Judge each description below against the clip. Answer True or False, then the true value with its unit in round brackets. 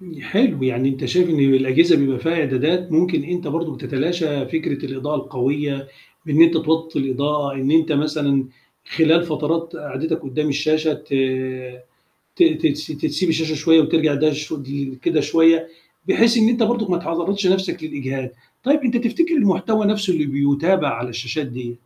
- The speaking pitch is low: False (155 Hz)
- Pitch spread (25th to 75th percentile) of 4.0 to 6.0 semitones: False (3.5 semitones)